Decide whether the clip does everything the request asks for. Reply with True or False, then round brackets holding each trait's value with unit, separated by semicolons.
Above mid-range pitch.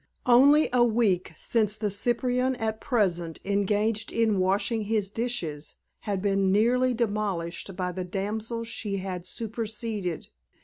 True (210 Hz)